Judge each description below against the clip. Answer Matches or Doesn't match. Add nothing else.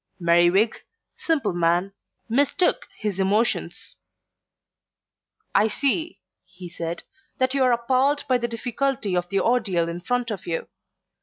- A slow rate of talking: Matches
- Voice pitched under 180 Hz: Doesn't match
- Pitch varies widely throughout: Matches